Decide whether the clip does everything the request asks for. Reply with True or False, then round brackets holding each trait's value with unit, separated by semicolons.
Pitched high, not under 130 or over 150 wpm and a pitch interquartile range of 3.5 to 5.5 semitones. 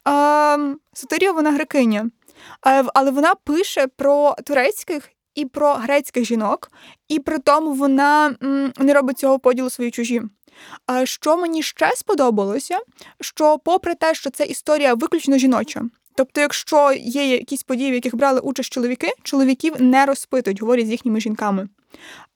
False (275 Hz; 140 wpm; 3.0 semitones)